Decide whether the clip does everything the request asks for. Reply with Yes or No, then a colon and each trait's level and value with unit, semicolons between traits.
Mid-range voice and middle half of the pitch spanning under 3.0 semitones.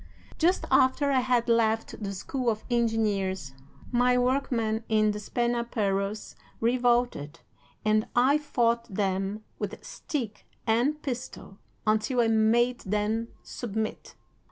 No: high, 230 Hz; narrow, 2.6 semitones